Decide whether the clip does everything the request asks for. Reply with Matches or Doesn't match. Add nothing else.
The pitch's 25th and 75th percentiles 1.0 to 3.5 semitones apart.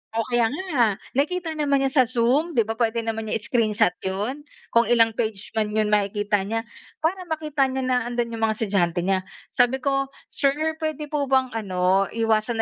Doesn't match